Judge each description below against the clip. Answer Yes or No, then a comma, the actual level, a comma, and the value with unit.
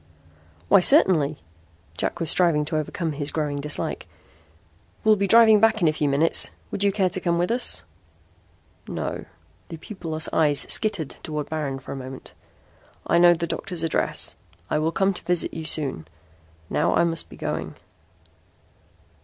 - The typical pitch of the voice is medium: Yes, medium, 165 Hz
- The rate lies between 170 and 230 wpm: No, average, 160 wpm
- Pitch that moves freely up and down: No, average, 3.7 semitones